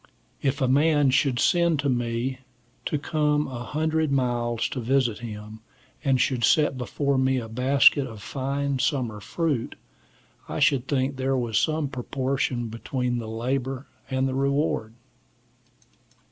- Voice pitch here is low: Yes, low, 130 Hz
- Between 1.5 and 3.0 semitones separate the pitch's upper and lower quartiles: Yes, average, 2.7 semitones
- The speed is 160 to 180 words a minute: No, average, 145 wpm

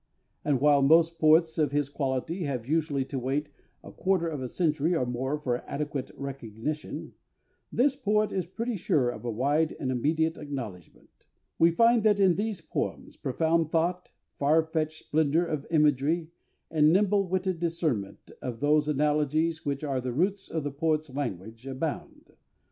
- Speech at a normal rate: Yes, average, 160 wpm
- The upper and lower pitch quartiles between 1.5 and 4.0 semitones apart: Yes, average, 3.4 semitones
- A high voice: No, medium, 155 Hz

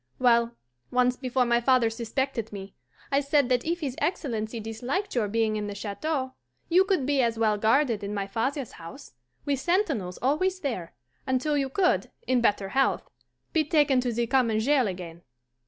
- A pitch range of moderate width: Yes, average, 4.3 semitones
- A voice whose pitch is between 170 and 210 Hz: No, very high, 250 Hz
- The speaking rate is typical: Yes, average, 175 wpm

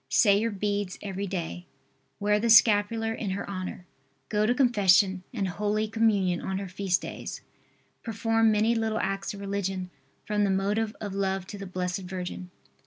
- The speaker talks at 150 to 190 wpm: Yes, average, 170 wpm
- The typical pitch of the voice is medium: No, high, 200 Hz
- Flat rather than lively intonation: Yes, narrow, 2.3 semitones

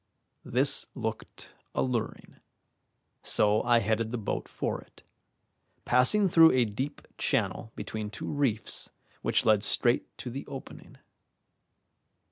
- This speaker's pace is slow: Yes, slow, 115 wpm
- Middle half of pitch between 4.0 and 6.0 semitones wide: No, average, 3.5 semitones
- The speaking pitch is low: Yes, low, 120 Hz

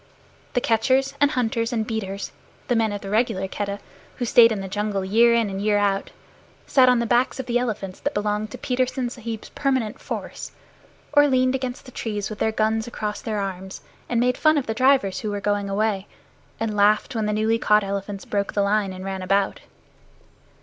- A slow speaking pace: No, fast, 205 wpm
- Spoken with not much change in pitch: No, average, 3.3 semitones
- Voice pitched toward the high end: Yes, high, 215 Hz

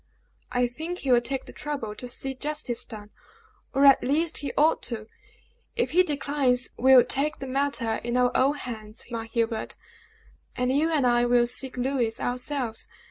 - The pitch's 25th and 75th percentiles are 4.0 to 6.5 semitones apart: No, average, 2.9 semitones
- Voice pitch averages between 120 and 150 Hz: No, very high, 255 Hz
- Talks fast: No, average, 180 wpm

